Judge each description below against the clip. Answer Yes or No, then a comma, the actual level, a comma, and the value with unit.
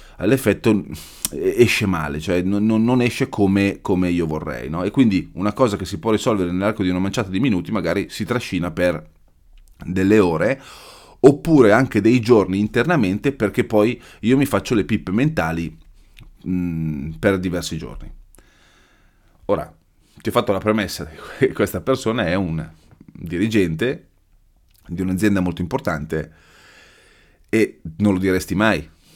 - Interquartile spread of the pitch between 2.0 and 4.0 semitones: Yes, average, 3.6 semitones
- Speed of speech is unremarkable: Yes, average, 145 wpm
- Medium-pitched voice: No, very low, 95 Hz